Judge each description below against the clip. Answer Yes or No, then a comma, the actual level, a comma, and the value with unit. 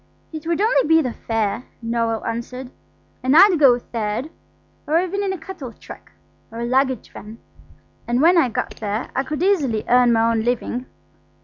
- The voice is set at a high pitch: Yes, very high, 250 Hz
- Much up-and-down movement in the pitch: Yes, wide, 5.8 semitones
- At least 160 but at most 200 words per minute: Yes, average, 180 wpm